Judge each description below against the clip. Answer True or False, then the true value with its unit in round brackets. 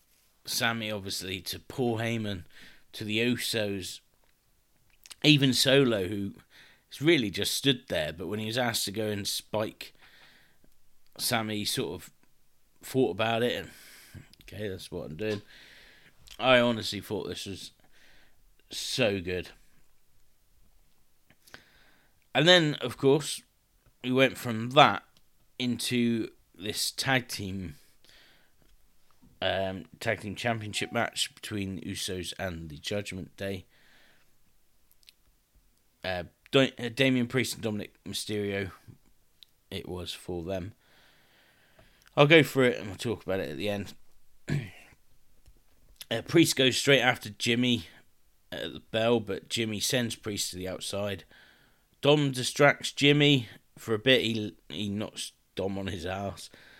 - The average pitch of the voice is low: True (110 Hz)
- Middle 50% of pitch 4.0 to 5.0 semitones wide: True (4.4 semitones)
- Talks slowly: True (125 wpm)